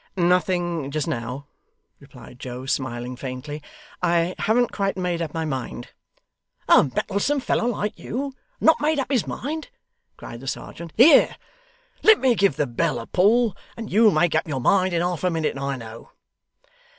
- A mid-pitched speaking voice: Yes, medium, 175 Hz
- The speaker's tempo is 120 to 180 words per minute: Yes, average, 170 wpm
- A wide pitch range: Yes, wide, 7.7 semitones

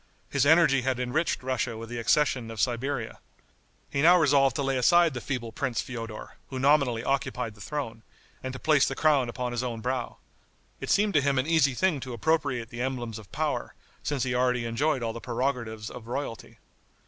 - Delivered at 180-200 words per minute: Yes, average, 195 wpm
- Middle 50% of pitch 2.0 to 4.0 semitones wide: Yes, average, 3.1 semitones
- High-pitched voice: No, low, 130 Hz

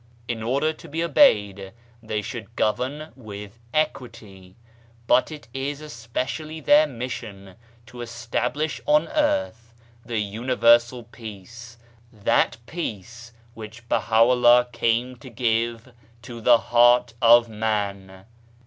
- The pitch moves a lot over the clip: No, narrow, 2.5 semitones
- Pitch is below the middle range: Yes, low, 120 Hz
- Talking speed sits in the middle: No, slow, 110 wpm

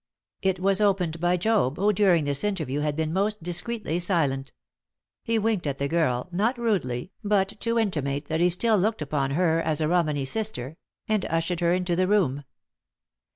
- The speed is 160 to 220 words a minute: Yes, average, 180 wpm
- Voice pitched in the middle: Yes, medium, 175 Hz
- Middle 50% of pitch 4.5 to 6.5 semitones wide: Yes, average, 5.2 semitones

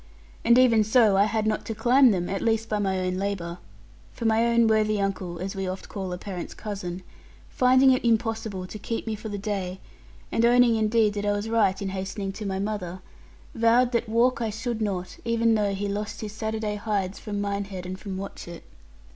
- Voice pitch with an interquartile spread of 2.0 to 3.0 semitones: Yes, average, 2.7 semitones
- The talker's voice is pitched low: No, high, 210 Hz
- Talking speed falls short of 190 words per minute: No, fast, 205 wpm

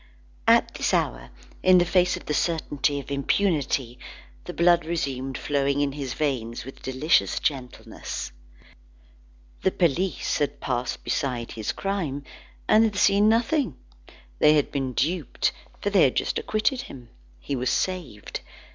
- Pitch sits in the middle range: Yes, medium, 145 Hz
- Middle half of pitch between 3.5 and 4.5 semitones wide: No, wide, 5.6 semitones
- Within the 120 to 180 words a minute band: Yes, average, 145 wpm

